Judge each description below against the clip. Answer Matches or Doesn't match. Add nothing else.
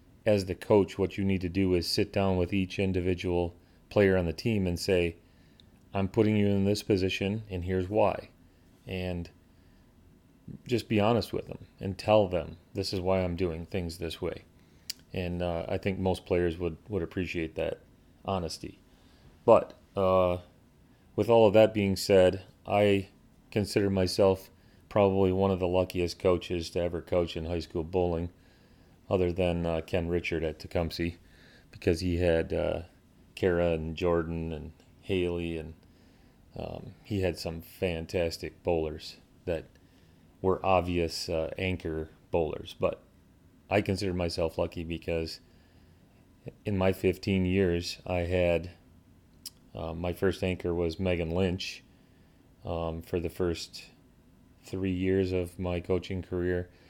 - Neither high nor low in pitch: Doesn't match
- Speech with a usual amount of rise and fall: Doesn't match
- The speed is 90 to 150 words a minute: Matches